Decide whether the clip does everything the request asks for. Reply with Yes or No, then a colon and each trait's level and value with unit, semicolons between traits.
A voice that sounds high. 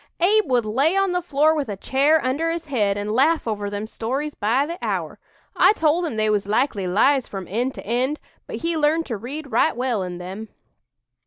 Yes: very high, 260 Hz